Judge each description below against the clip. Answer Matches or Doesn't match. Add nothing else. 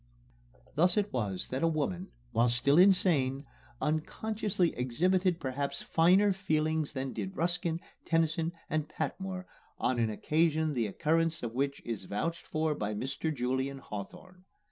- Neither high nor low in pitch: Matches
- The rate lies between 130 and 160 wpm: Matches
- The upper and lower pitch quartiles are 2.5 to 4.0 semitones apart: Doesn't match